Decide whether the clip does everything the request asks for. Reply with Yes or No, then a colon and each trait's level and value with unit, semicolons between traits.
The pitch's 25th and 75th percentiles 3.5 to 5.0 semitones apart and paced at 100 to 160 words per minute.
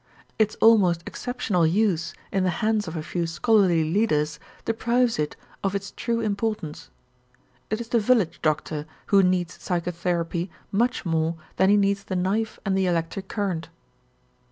Yes: average, 4.4 semitones; average, 155 wpm